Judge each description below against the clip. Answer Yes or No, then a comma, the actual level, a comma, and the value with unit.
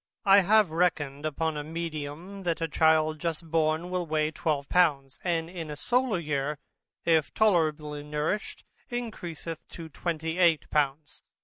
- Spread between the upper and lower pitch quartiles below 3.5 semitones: Yes, narrow, 2.6 semitones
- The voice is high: No, medium, 160 Hz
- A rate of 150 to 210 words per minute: No, average, 140 wpm